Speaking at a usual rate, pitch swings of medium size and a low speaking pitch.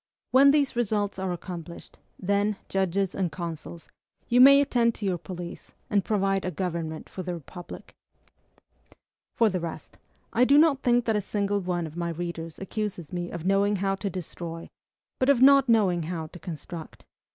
No: average, 175 wpm; average, 4.1 semitones; high, 190 Hz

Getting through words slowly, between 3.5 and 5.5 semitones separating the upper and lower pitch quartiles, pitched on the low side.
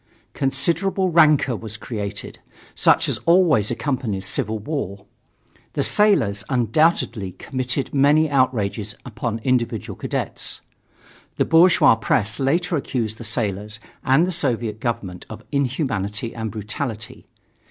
Yes: slow, 115 wpm; average, 5.2 semitones; low, 120 Hz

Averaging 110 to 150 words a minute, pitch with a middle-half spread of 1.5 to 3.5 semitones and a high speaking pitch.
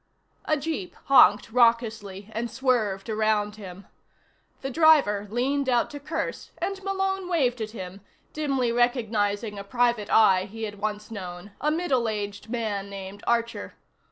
No: average, 145 wpm; average, 4.2 semitones; high, 225 Hz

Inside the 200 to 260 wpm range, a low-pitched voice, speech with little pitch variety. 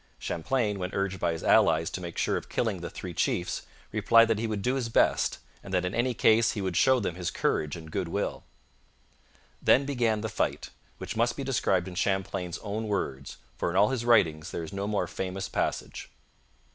No: fast, 205 wpm; low, 100 Hz; average, 4.3 semitones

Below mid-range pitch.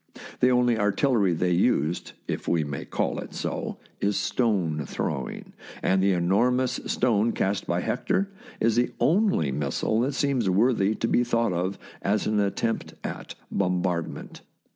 Yes: low, 100 Hz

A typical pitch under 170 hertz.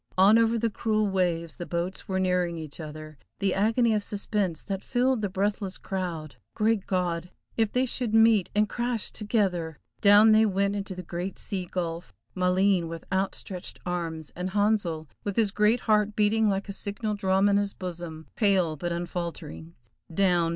No: high, 195 Hz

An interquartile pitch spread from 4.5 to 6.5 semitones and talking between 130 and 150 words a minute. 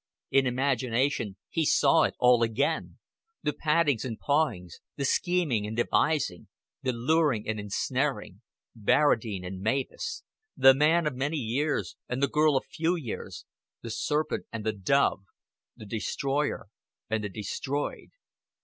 Yes: average, 5.1 semitones; average, 140 wpm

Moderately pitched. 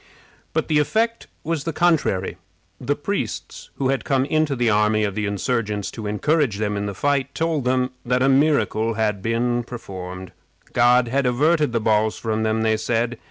No: low, 120 Hz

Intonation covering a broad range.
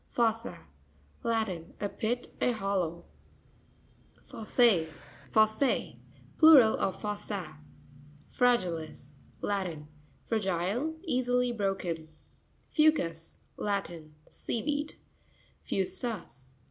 Yes: wide, 6.3 semitones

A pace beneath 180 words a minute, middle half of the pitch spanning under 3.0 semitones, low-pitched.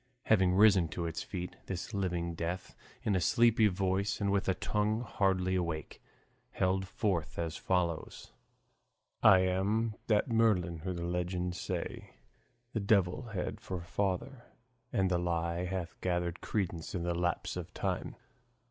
Yes: average, 150 wpm; narrow, 2.4 semitones; very low, 95 Hz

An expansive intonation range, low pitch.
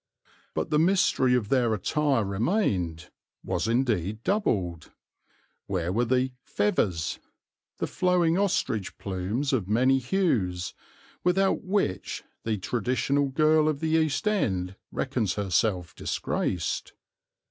Yes: wide, 8.2 semitones; low, 120 Hz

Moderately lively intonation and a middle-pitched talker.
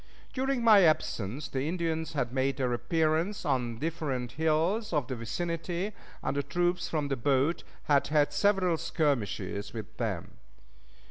Yes: average, 4.8 semitones; medium, 150 Hz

